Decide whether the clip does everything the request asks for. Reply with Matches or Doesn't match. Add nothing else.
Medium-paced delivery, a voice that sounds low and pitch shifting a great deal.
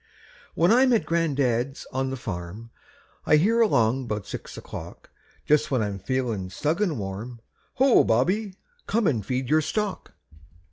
Matches